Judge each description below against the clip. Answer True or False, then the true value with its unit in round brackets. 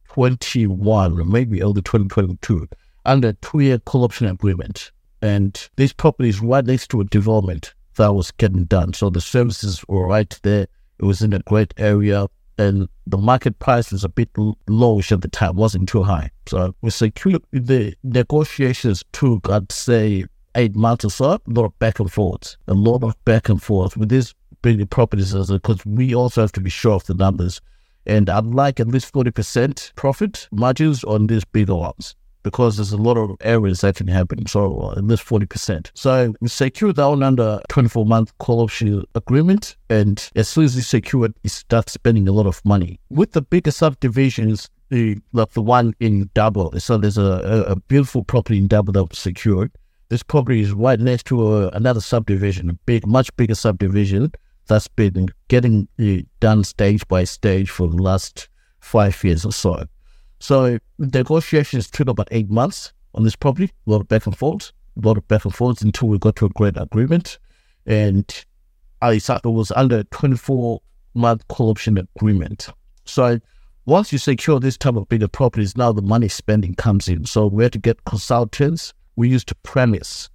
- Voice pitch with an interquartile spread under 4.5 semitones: True (3.6 semitones)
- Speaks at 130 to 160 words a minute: False (185 wpm)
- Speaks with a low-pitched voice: True (110 Hz)